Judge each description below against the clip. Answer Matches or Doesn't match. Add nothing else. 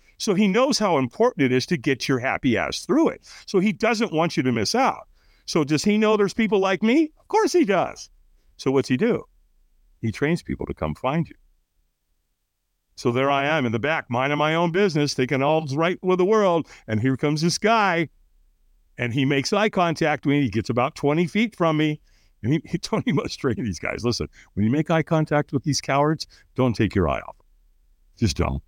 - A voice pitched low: Doesn't match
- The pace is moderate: Doesn't match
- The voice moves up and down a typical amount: Doesn't match